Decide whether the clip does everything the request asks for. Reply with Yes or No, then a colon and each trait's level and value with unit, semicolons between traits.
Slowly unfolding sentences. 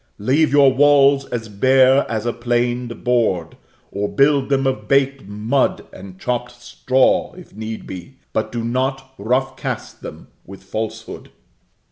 No: average, 145 wpm